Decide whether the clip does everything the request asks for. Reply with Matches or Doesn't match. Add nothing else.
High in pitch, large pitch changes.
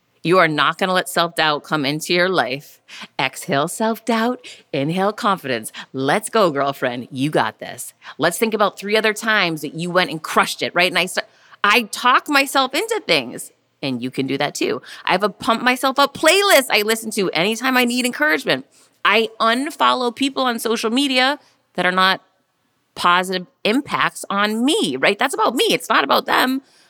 Matches